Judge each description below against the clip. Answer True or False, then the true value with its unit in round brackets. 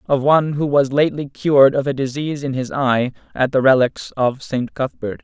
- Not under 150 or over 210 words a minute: True (205 wpm)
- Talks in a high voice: False (135 Hz)